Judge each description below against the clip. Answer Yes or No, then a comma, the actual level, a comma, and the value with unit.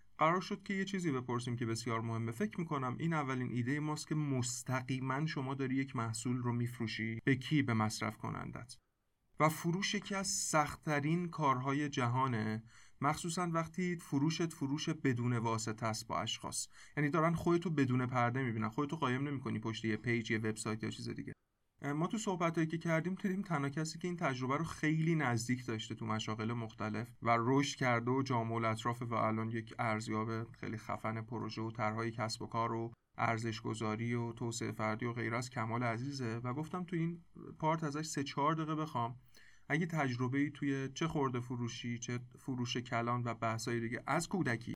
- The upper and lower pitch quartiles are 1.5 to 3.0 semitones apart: No, average, 4.9 semitones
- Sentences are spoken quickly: Yes, fast, 180 wpm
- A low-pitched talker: Yes, low, 125 Hz